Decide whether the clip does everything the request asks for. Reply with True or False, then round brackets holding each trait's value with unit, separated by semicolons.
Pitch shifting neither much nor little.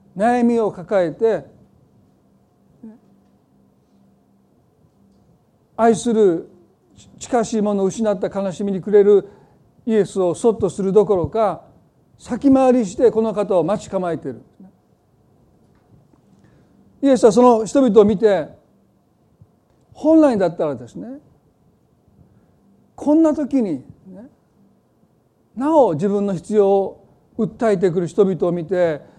True (3.7 semitones)